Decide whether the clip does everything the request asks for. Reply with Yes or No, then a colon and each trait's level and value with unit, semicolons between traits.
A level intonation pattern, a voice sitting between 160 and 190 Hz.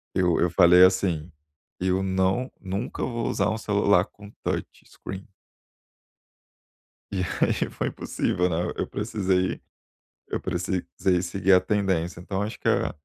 No: narrow, 2.1 semitones; very low, 95 Hz